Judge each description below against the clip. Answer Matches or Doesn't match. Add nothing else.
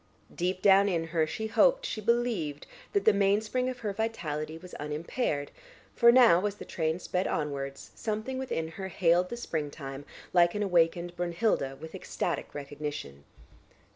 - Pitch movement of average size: Doesn't match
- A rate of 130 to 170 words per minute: Matches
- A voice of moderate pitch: Matches